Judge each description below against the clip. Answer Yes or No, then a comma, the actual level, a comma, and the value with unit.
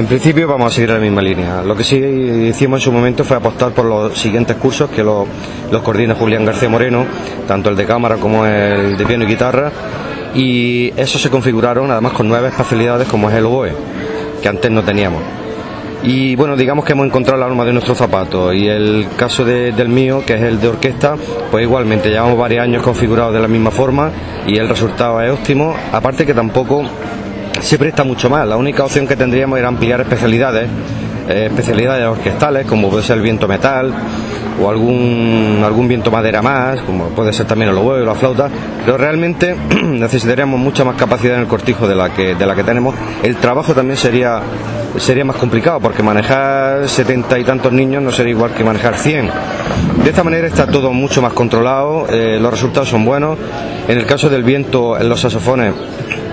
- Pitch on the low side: Yes, low, 120 Hz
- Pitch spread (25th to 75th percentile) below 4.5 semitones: Yes, average, 2.9 semitones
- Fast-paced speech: Yes, fast, 200 wpm